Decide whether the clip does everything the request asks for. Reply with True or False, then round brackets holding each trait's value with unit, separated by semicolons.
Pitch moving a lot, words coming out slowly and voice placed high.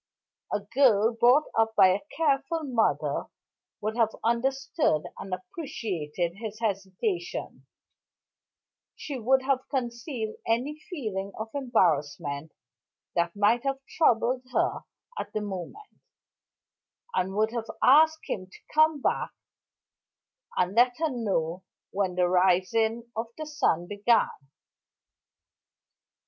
True (5.8 semitones; 115 wpm; 225 Hz)